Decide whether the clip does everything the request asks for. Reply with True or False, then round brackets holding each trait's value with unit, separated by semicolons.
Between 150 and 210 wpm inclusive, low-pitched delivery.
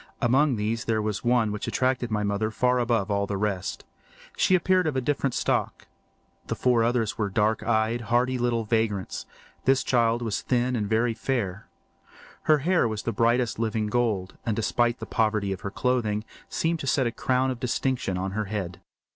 True (190 wpm; 115 Hz)